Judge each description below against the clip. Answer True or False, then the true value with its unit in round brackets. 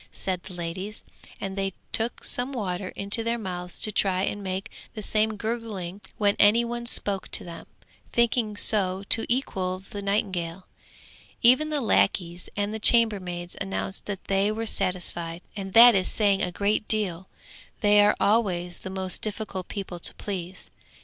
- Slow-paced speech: False (165 wpm)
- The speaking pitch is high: True (200 Hz)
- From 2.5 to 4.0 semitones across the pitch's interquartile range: True (2.9 semitones)